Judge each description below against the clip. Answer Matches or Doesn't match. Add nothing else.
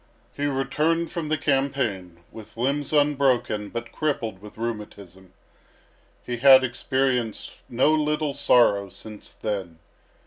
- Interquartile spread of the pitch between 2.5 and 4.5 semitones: Doesn't match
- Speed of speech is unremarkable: Doesn't match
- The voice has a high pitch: Doesn't match